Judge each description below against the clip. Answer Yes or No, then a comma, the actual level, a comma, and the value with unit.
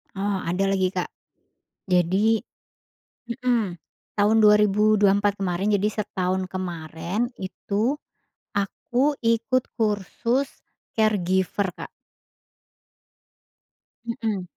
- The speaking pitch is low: No, high, 205 Hz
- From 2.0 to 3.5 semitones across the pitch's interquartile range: Yes, average, 2.9 semitones